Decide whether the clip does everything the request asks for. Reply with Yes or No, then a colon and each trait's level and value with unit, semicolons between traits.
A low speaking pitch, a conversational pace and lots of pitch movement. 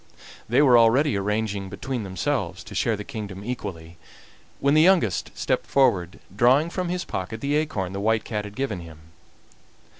Yes: low, 110 Hz; average, 170 wpm; wide, 5.7 semitones